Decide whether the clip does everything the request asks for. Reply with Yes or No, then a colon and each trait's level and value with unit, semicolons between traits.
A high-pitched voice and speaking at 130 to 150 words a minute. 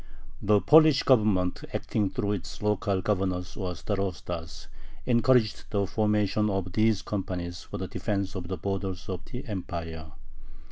No: low, 100 Hz; average, 140 wpm